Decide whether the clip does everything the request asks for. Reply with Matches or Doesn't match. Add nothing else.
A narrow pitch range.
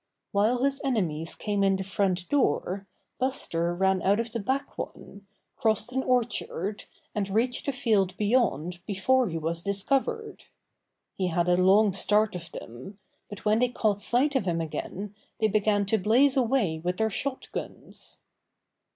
Doesn't match